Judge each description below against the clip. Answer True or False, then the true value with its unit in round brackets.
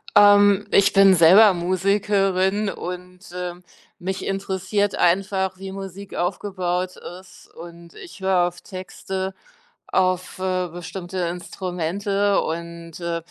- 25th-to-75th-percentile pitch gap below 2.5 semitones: True (1.8 semitones)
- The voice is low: False (185 Hz)